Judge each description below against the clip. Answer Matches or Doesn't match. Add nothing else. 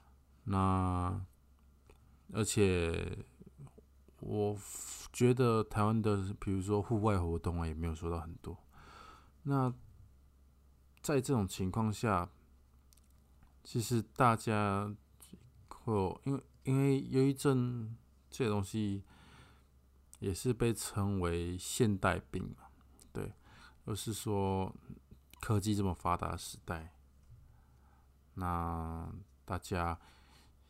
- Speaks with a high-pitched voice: Doesn't match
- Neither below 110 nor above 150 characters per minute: Matches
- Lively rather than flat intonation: Matches